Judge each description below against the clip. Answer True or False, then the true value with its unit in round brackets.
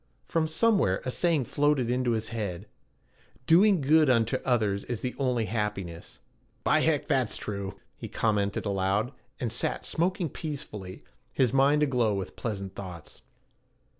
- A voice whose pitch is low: True (120 Hz)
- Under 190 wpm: True (140 wpm)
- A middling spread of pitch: False (6.4 semitones)